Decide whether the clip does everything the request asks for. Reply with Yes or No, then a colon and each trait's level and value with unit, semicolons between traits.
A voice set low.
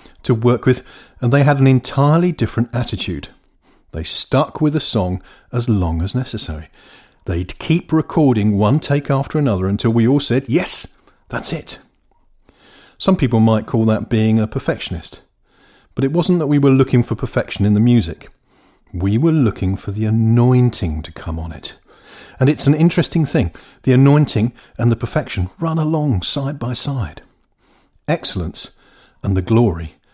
Yes: low, 120 Hz